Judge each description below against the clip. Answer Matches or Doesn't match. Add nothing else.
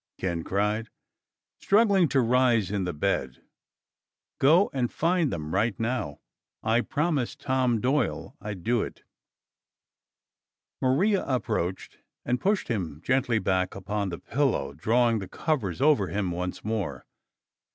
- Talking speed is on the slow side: Matches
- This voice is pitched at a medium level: Doesn't match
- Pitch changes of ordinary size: Doesn't match